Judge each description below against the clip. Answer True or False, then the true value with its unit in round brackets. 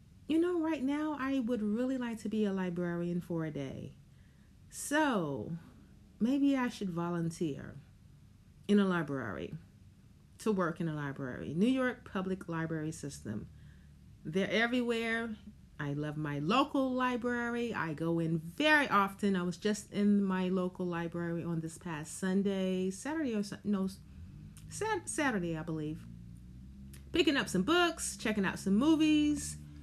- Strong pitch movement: True (7.0 semitones)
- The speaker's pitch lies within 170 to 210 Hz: True (190 Hz)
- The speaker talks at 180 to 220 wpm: False (140 wpm)